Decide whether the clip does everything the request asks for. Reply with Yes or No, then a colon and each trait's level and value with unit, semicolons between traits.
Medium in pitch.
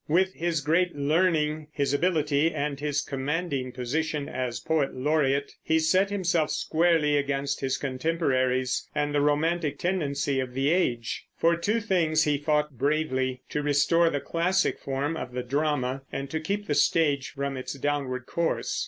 Yes: medium, 150 Hz